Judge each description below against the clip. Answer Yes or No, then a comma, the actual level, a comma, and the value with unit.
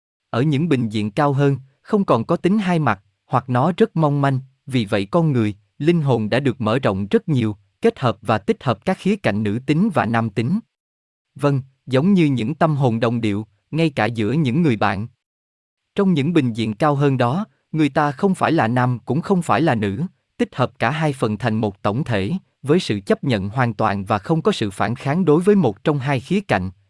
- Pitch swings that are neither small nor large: No, wide, 6.6 semitones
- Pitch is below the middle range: Yes, low, 130 Hz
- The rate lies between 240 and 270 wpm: No, average, 230 wpm